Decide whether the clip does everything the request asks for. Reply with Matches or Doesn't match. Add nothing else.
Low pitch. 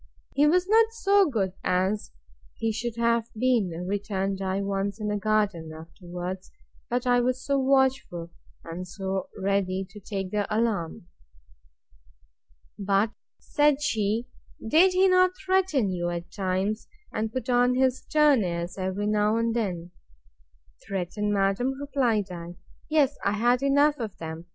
Doesn't match